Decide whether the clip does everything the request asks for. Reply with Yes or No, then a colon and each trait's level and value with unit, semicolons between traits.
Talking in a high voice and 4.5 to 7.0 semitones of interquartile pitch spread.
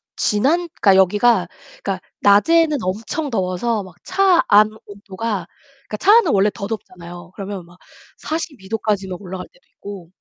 No: high, 205 Hz; average, 3.9 semitones